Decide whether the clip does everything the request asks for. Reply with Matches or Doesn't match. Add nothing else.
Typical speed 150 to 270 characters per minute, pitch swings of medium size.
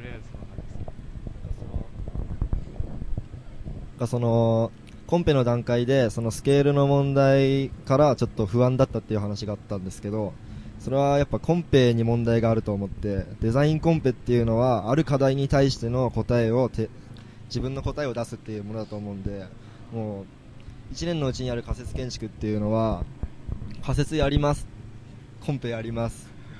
Doesn't match